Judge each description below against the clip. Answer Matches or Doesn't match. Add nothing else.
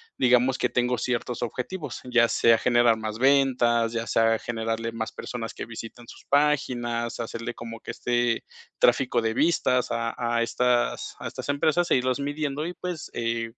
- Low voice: Matches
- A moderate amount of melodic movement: Doesn't match